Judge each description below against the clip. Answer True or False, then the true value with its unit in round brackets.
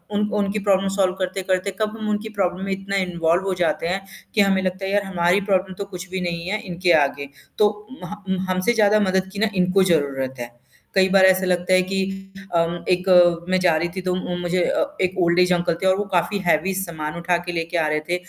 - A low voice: False (185 Hz)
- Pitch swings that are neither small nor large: False (2.0 semitones)